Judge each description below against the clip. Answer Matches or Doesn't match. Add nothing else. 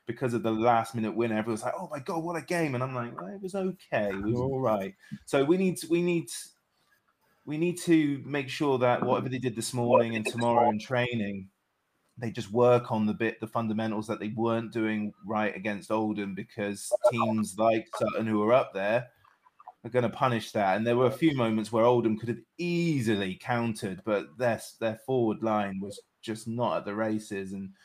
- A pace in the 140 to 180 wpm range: Doesn't match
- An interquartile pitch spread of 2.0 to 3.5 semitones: Matches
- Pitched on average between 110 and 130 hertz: Matches